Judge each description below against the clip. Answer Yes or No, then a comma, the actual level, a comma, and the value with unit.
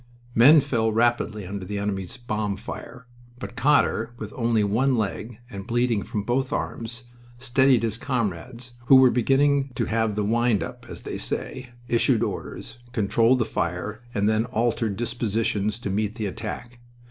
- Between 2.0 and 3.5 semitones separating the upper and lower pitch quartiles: Yes, average, 2.8 semitones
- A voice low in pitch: Yes, low, 115 Hz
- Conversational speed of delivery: Yes, average, 160 wpm